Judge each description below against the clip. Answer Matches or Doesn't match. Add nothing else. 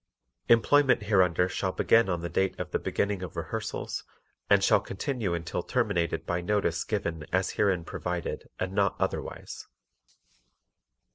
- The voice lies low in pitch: Matches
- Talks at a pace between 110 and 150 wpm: Matches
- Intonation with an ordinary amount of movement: Matches